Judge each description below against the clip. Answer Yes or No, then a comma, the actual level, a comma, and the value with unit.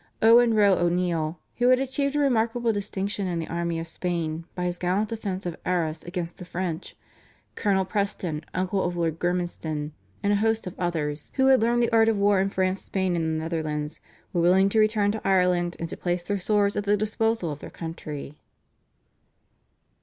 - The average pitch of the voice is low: No, medium, 185 Hz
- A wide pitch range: No, average, 3.7 semitones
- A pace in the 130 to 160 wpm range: No, average, 190 wpm